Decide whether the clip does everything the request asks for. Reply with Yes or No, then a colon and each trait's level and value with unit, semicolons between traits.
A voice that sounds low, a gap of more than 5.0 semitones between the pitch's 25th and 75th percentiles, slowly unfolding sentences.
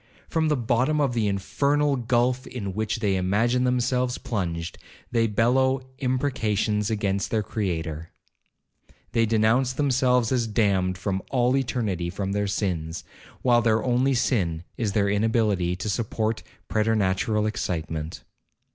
No: low, 110 Hz; average, 4.1 semitones; slow, 130 wpm